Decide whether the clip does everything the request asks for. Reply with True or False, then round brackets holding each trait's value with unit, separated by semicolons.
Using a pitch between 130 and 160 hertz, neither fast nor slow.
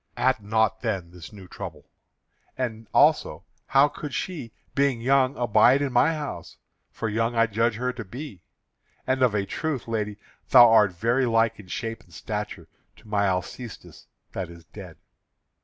False (115 Hz; 165 wpm)